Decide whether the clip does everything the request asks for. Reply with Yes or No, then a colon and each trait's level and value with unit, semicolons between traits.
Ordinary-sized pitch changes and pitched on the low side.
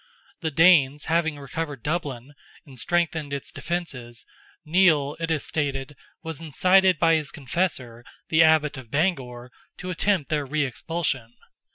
No: average, 3.5 semitones; medium, 150 Hz